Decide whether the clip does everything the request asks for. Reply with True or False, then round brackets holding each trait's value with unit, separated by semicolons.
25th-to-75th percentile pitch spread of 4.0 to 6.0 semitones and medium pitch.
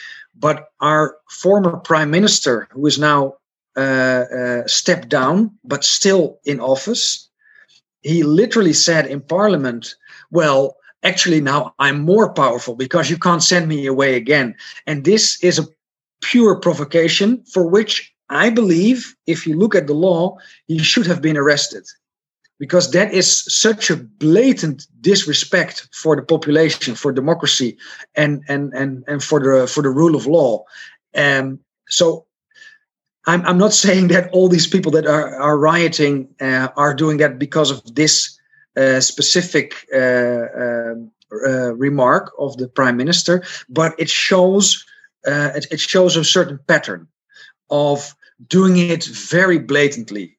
True (4.6 semitones; 155 Hz)